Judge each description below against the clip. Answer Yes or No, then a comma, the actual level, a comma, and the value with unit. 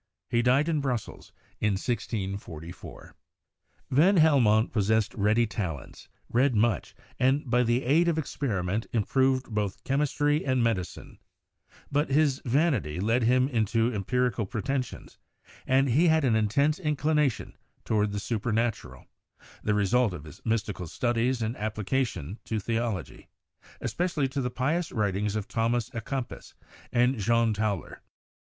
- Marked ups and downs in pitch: No, average, 4.1 semitones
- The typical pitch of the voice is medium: No, low, 120 Hz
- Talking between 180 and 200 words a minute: No, average, 140 wpm